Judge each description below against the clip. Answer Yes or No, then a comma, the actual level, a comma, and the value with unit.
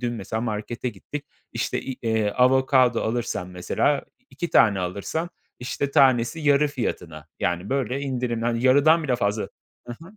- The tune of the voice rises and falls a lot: No, average, 4.0 semitones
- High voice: No, low, 120 Hz